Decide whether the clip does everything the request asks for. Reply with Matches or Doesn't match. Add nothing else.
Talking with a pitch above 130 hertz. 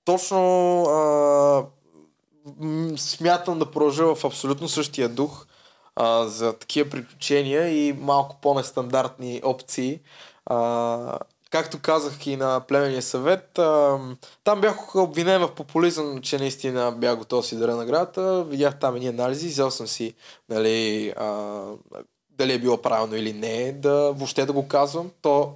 Matches